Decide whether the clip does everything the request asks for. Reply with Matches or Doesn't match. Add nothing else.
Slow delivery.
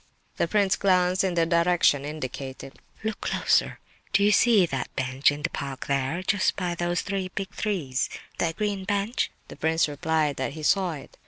Doesn't match